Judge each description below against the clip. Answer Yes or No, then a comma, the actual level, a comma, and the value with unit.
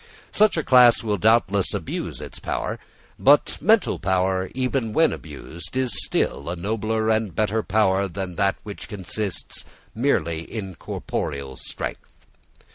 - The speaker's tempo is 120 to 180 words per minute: Yes, slow, 135 wpm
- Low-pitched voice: Yes, low, 105 Hz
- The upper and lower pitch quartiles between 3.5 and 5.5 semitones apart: Yes, average, 3.8 semitones